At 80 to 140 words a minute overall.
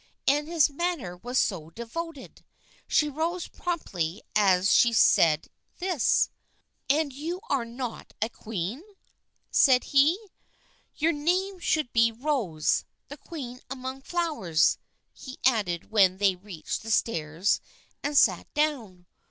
Yes: slow, 135 wpm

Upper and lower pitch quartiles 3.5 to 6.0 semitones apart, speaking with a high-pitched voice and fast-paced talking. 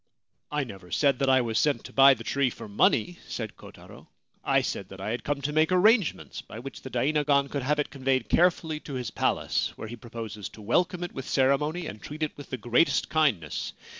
No: average, 4.3 semitones; medium, 140 Hz; fast, 225 wpm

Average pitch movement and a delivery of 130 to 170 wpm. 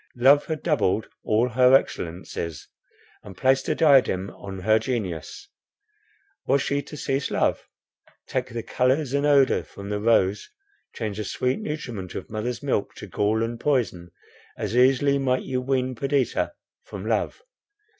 Yes: average, 4.5 semitones; average, 155 wpm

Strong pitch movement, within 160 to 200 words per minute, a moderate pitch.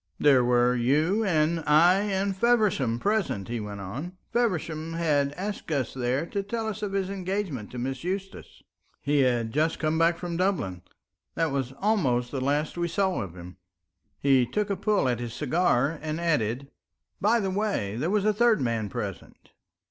Yes: wide, 7.6 semitones; average, 180 wpm; medium, 160 Hz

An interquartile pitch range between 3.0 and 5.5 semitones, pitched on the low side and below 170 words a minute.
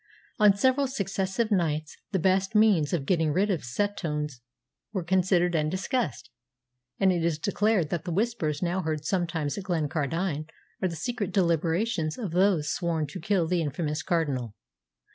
No: average, 4.0 semitones; medium, 175 Hz; average, 160 wpm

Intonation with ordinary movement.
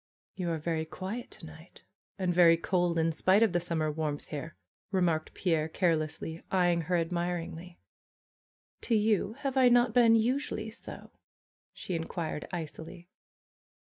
Yes: average, 3.3 semitones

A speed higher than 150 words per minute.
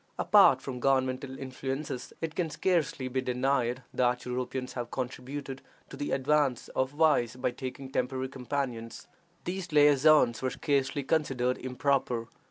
No: slow, 135 wpm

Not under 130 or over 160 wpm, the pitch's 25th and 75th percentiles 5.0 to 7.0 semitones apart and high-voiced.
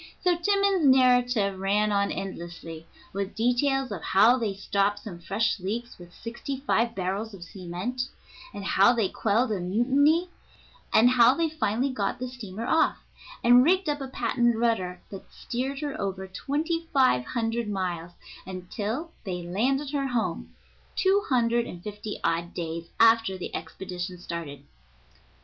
Yes: average, 150 wpm; wide, 5.4 semitones; high, 225 Hz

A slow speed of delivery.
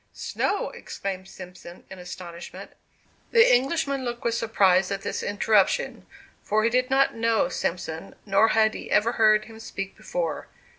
No: average, 150 wpm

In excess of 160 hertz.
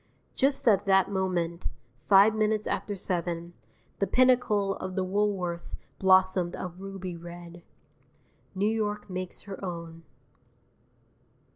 Yes: high, 190 Hz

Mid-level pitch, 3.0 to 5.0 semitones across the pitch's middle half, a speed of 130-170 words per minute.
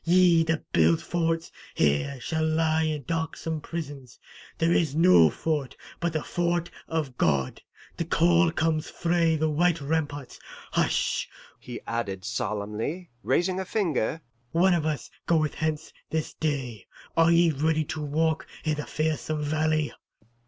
No: medium, 155 Hz; narrow, 2.5 semitones; average, 145 wpm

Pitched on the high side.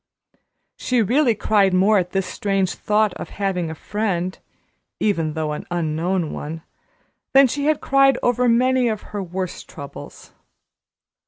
Yes: high, 195 Hz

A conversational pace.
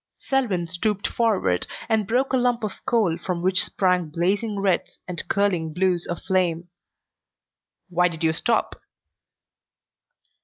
No: slow, 130 wpm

